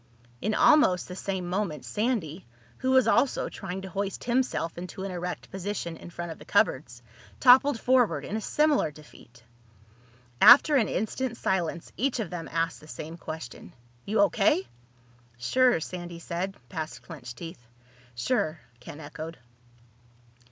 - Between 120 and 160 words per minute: Yes, average, 145 wpm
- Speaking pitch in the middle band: Yes, medium, 180 Hz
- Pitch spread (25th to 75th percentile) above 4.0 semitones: Yes, wide, 5.6 semitones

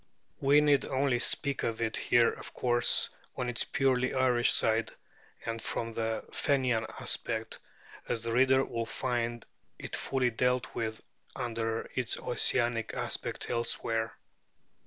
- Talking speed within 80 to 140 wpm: Yes, slow, 135 wpm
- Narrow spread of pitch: Yes, narrow, 2.1 semitones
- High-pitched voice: No, low, 120 Hz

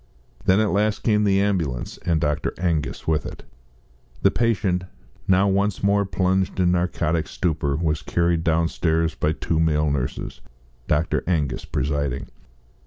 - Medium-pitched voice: No, very low, 85 Hz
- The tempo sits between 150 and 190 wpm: No, average, 140 wpm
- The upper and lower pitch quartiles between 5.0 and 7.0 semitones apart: No, average, 3.9 semitones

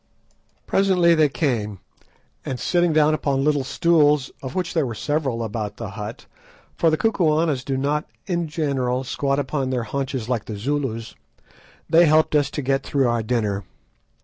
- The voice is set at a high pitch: No, medium, 140 Hz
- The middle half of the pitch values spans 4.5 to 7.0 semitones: No, average, 4.0 semitones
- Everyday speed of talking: Yes, average, 165 wpm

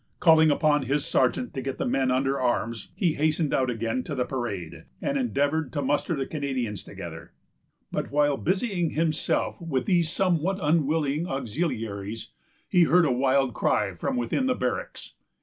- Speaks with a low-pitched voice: No, medium, 145 Hz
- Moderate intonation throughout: Yes, average, 4.2 semitones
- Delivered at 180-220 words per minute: No, average, 165 wpm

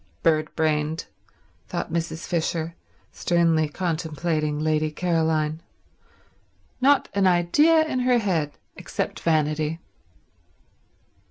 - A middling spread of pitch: No, narrow, 2.1 semitones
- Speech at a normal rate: No, slow, 90 wpm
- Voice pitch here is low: No, medium, 160 Hz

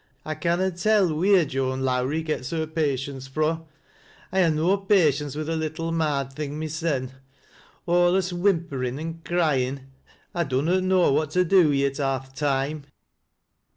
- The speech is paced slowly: No, average, 155 wpm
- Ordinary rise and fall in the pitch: Yes, average, 3.9 semitones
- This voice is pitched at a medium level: Yes, medium, 155 Hz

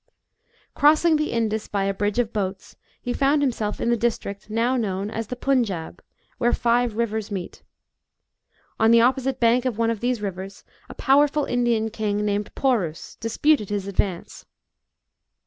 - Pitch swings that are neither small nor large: Yes, average, 3.2 semitones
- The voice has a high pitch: Yes, high, 230 Hz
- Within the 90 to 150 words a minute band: No, average, 160 wpm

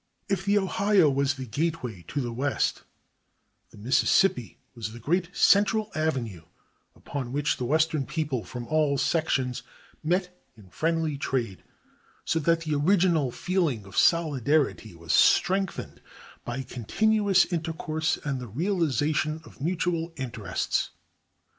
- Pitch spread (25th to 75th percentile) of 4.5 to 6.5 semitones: Yes, average, 5.1 semitones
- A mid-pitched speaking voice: Yes, medium, 155 Hz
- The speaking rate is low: Yes, slow, 130 wpm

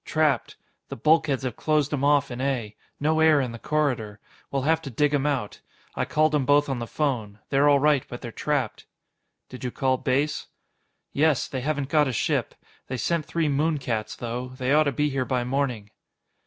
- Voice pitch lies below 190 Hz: Yes, medium, 140 Hz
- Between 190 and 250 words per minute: Yes, fast, 205 wpm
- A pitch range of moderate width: Yes, average, 3.0 semitones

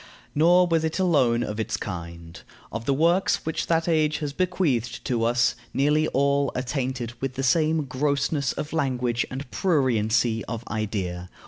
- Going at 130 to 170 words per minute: Yes, average, 160 wpm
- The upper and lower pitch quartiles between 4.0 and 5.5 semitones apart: Yes, average, 4.9 semitones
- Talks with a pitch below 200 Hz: Yes, low, 135 Hz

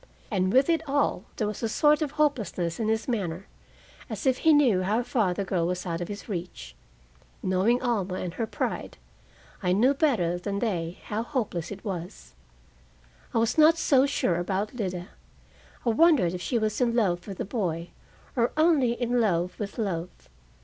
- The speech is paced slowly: No, average, 185 wpm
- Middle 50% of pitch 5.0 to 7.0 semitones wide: Yes, wide, 5.4 semitones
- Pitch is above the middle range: Yes, high, 210 Hz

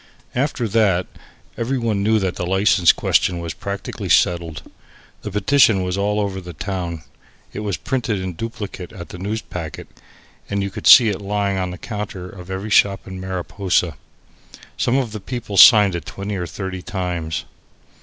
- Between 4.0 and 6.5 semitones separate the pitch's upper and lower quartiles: No, average, 2.7 semitones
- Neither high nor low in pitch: No, low, 100 Hz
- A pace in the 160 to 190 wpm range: Yes, average, 170 wpm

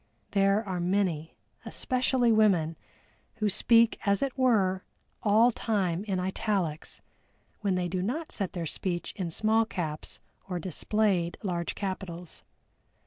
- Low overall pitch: No, high, 195 Hz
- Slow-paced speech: Yes, slow, 130 wpm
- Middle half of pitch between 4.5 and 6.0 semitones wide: No, average, 3.7 semitones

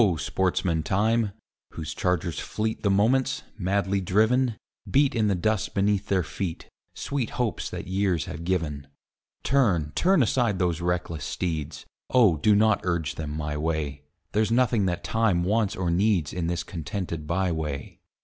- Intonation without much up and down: No, average, 4.8 semitones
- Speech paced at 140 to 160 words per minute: Yes, average, 155 wpm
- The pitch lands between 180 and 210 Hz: No, very low, 95 Hz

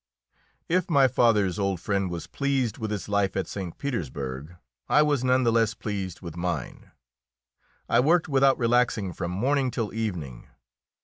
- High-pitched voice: No, low, 110 Hz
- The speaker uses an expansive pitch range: Yes, wide, 5.9 semitones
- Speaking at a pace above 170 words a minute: No, average, 160 wpm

